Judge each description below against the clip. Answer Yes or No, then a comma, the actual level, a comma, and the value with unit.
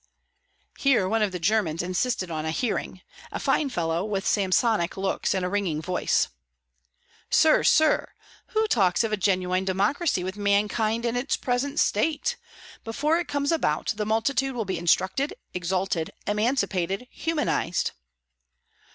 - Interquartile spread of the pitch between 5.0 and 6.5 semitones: Yes, average, 5.3 semitones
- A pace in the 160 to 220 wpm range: No, average, 145 wpm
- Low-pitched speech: No, high, 205 Hz